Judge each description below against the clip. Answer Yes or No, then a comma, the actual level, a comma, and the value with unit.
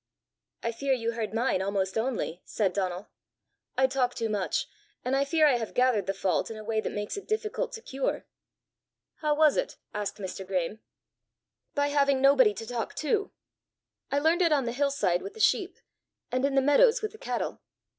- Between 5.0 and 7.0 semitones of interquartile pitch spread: Yes, wide, 5.6 semitones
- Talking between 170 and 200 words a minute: Yes, average, 195 wpm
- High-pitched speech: Yes, very high, 255 Hz